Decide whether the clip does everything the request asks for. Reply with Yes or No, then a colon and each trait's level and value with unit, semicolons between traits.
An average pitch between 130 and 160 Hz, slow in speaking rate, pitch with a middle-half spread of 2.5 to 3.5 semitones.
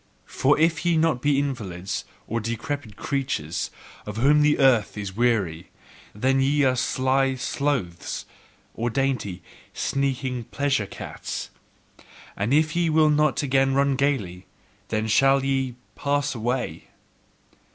No: low, 135 Hz; slow, 130 wpm; average, 4.2 semitones